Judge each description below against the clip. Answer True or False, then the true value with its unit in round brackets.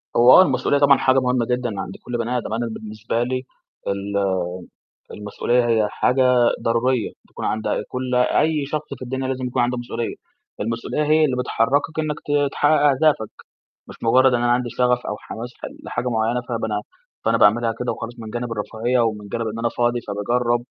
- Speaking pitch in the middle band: False (120 Hz)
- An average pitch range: False (2.2 semitones)